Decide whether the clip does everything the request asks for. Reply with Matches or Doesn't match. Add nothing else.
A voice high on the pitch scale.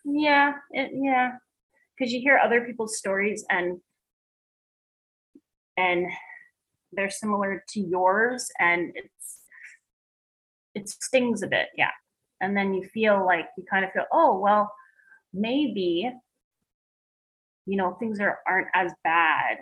Matches